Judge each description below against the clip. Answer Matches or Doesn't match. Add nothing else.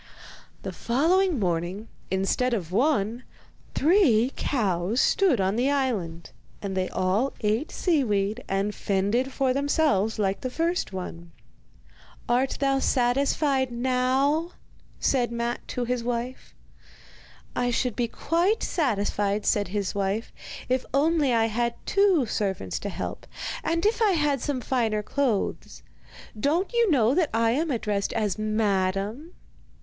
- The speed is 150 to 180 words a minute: Doesn't match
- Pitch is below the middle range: Doesn't match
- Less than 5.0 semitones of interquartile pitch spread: Doesn't match